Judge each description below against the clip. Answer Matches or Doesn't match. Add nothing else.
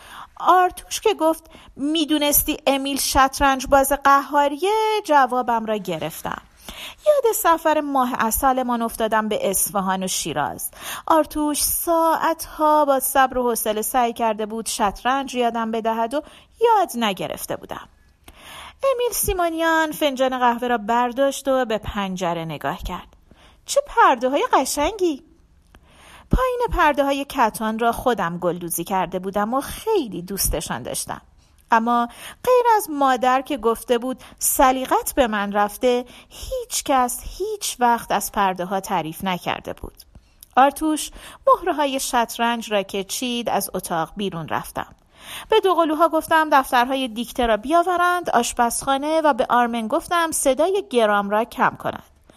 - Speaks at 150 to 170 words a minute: Doesn't match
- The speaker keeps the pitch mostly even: Doesn't match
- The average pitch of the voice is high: Matches